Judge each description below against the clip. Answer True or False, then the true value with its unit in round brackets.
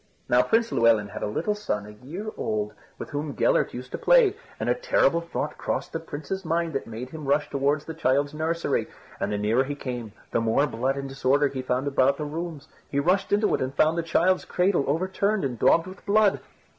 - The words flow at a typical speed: False (220 wpm)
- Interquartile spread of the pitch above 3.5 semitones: True (5.0 semitones)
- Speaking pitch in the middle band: True (145 Hz)